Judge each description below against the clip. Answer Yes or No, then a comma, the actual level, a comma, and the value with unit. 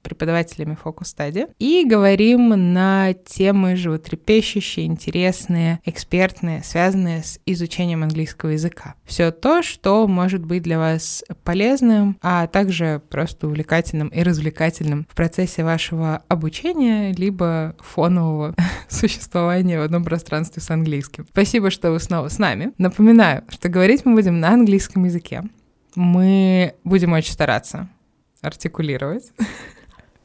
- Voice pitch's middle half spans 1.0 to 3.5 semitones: Yes, average, 3.1 semitones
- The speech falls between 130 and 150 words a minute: No, average, 120 wpm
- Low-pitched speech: No, medium, 175 Hz